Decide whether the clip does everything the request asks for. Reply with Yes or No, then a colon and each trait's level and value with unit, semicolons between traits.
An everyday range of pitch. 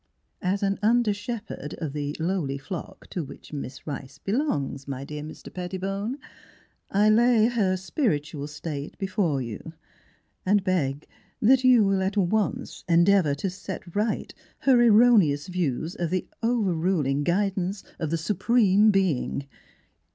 No: wide, 5.7 semitones